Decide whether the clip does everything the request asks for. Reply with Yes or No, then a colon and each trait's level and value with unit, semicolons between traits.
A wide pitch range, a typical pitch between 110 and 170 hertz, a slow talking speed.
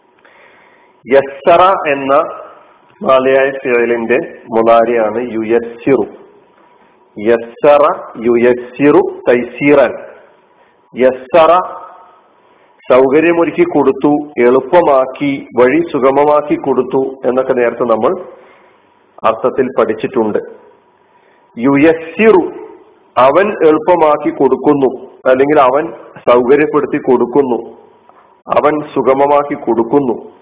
No: average, 5.0 semitones; medium, 140 Hz; slow, 55 wpm